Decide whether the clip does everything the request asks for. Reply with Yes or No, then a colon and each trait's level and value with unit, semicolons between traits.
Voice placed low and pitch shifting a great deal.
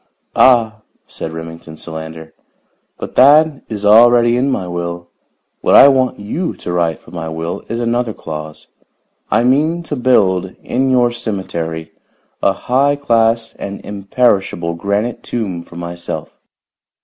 Yes: low, 105 Hz; wide, 6.2 semitones